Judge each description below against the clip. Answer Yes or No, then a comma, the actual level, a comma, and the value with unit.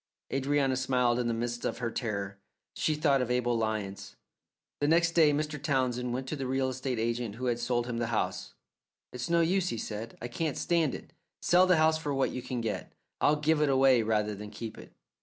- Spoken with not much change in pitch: No, average, 4.0 semitones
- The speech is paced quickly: Yes, fast, 215 wpm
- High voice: No, low, 125 Hz